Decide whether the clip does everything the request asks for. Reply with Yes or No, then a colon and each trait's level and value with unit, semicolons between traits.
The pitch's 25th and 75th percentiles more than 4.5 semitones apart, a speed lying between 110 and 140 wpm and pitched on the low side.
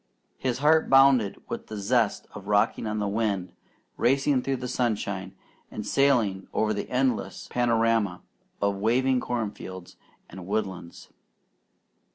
No: average, 4.1 semitones; slow, 135 wpm; low, 110 Hz